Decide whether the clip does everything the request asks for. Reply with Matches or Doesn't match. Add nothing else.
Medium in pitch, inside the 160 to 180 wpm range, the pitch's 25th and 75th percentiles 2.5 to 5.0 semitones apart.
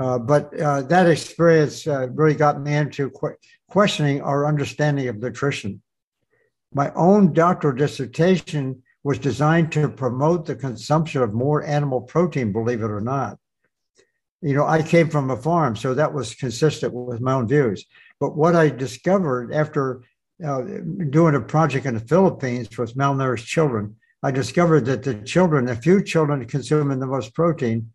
Matches